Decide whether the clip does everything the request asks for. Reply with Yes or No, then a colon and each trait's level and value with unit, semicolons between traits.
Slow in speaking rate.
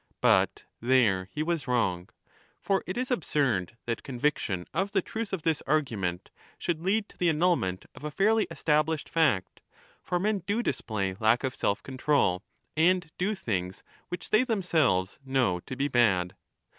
No: average, 165 wpm